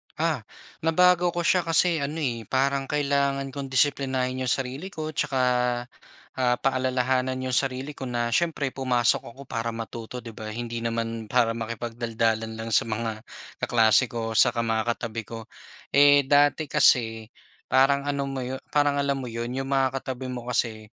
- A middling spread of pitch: Yes, average, 3.2 semitones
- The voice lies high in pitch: No, low, 130 Hz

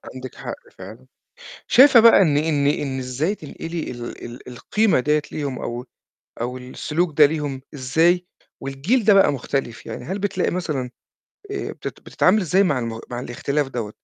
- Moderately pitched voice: Yes, medium, 145 Hz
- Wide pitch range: Yes, wide, 5.7 semitones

